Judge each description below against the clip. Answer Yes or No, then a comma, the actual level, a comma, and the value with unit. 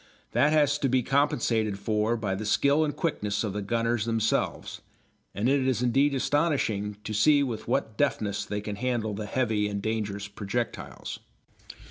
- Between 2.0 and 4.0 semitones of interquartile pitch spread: No, average, 4.5 semitones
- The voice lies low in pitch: Yes, low, 115 Hz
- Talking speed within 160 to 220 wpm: Yes, average, 165 wpm